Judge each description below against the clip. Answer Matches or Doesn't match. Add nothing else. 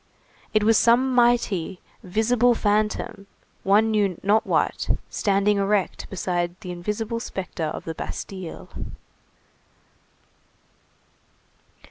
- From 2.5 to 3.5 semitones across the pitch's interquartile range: Matches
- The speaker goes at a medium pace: Doesn't match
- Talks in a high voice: Matches